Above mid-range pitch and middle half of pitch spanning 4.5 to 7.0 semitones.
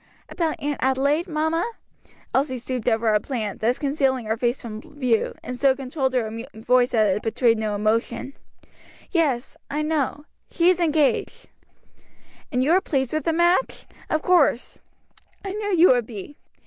Yes: very high, 265 Hz; average, 4.9 semitones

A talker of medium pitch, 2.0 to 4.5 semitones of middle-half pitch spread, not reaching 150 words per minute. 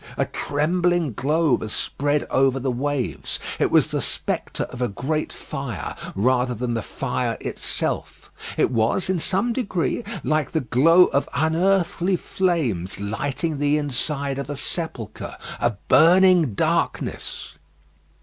No: medium, 145 Hz; average, 5.1 semitones; slow, 135 wpm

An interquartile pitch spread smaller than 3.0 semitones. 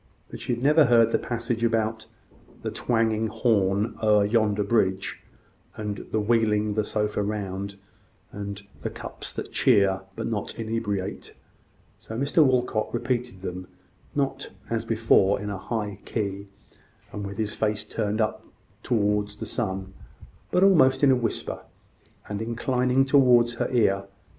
Yes: narrow, 2.6 semitones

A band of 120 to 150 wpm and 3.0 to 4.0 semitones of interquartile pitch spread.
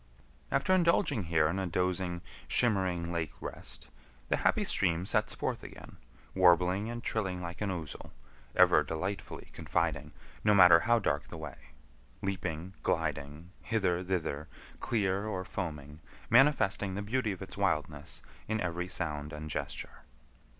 Yes: average, 140 wpm; average, 3.6 semitones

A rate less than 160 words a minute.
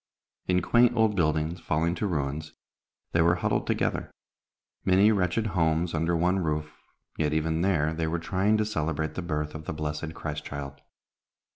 No: average, 165 wpm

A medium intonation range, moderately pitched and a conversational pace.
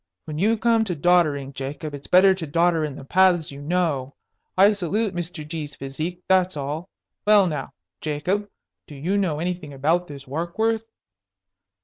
Yes: average, 4.2 semitones; medium, 170 Hz; average, 160 wpm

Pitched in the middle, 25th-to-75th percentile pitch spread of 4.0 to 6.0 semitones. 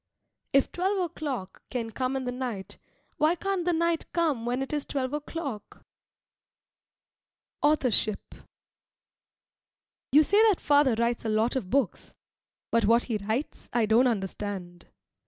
No: very high, 255 Hz; average, 5.2 semitones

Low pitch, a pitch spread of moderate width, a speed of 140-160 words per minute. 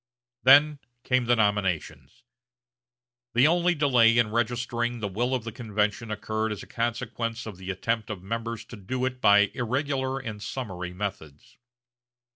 Yes: low, 115 Hz; average, 3.4 semitones; average, 150 wpm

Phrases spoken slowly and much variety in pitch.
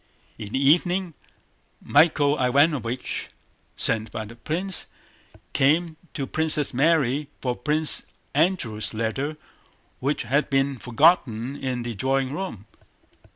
No: slow, 110 wpm; average, 4.2 semitones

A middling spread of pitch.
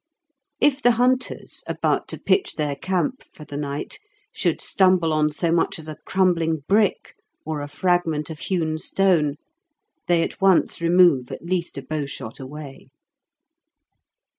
Yes: average, 3.8 semitones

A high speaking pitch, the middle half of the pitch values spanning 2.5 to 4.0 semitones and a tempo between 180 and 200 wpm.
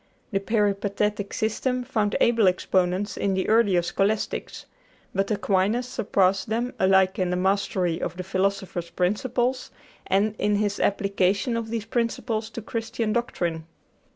No: high, 205 Hz; average, 2.9 semitones; slow, 135 wpm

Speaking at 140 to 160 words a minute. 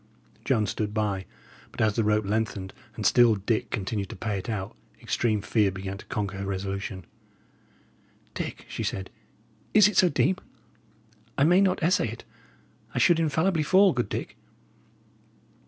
Yes: average, 155 wpm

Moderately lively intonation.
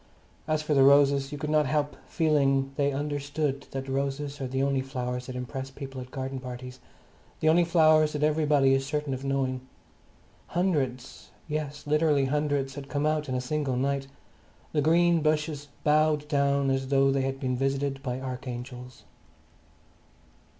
No: narrow, 2.1 semitones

